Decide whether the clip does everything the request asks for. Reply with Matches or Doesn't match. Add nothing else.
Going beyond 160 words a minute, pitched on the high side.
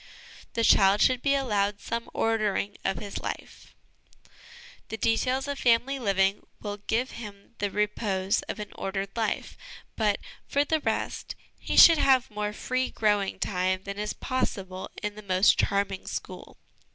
Doesn't match